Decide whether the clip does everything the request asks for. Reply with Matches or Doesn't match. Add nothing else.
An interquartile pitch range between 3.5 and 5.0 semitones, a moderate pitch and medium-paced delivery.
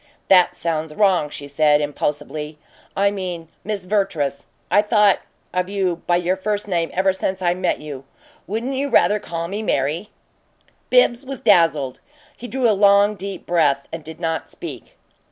Matches